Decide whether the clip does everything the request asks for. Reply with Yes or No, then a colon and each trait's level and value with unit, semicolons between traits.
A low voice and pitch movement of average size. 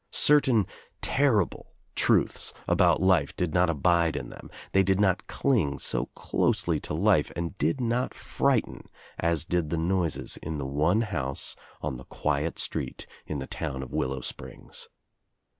Yes: very low, 85 Hz; average, 4.6 semitones